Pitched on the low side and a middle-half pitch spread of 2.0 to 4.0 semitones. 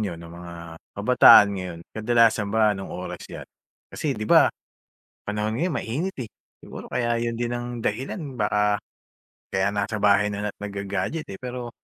Yes: low, 105 Hz; average, 2.9 semitones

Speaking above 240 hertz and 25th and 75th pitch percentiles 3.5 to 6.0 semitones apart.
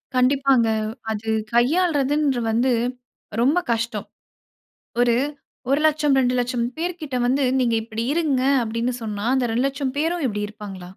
Yes: very high, 255 Hz; average, 3.8 semitones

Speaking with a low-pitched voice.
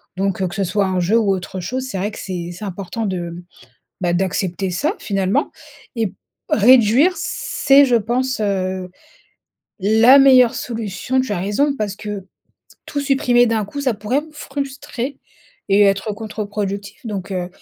No: high, 210 Hz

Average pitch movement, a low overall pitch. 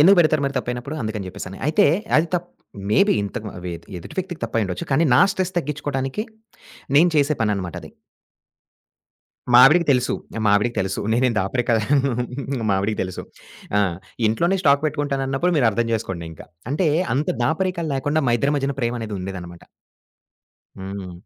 No: wide, 6.8 semitones; low, 130 Hz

